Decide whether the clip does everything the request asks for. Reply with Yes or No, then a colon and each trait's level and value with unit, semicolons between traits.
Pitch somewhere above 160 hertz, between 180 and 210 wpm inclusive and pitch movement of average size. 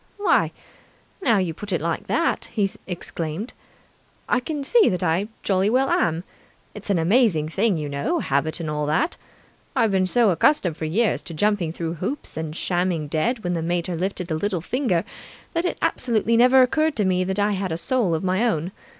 No: medium, 185 Hz; average, 195 wpm; wide, 5.8 semitones